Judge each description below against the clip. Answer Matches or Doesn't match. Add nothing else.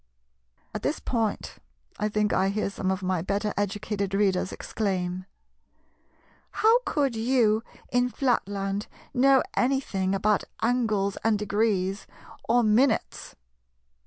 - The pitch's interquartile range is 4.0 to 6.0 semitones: Doesn't match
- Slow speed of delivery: Matches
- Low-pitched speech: Doesn't match